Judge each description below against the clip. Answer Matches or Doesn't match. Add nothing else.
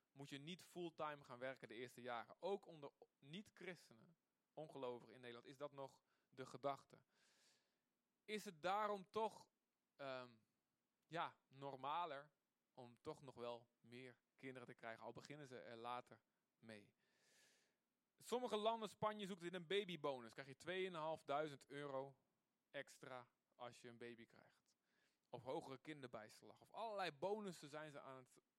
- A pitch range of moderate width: Doesn't match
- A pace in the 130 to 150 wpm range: Matches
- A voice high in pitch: Doesn't match